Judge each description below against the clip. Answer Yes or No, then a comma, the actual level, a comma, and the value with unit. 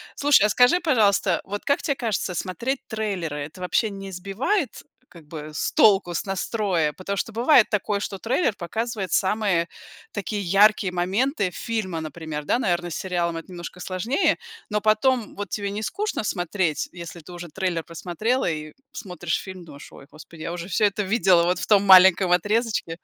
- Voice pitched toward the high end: Yes, high, 195 Hz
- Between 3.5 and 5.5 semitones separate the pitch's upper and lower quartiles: Yes, average, 3.9 semitones